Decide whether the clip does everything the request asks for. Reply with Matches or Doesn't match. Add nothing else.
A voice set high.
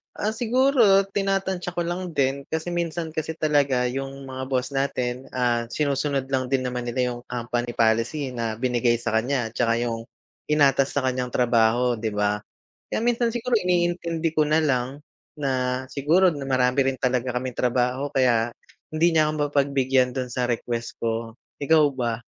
Doesn't match